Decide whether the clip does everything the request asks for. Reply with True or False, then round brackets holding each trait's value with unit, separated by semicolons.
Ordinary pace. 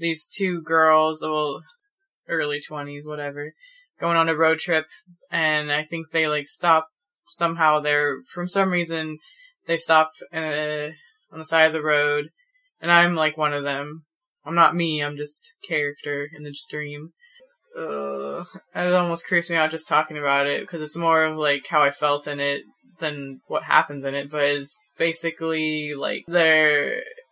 True (170 wpm)